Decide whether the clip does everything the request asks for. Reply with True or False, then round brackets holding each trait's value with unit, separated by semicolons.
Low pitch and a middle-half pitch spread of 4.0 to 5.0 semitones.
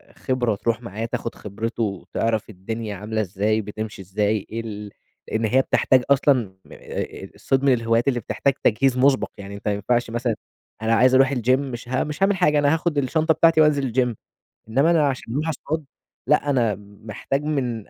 True (120 Hz; 4.3 semitones)